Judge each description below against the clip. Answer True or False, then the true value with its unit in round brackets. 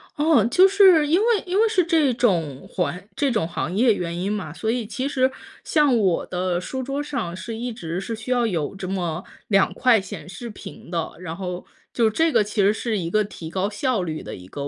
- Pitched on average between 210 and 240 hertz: True (215 Hz)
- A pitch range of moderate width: False (6.3 semitones)